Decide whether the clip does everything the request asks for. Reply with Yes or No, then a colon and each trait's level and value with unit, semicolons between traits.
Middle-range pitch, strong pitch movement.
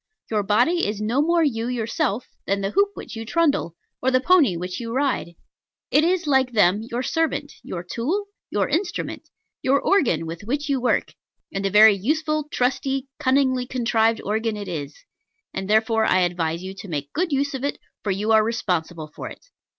No: high, 230 Hz; wide, 6.2 semitones